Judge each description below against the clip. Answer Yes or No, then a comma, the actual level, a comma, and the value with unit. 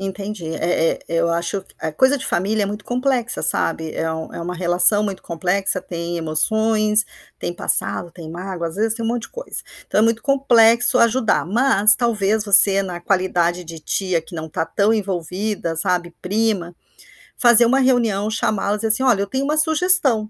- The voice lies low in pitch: No, high, 200 Hz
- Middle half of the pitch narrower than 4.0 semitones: No, average, 4.7 semitones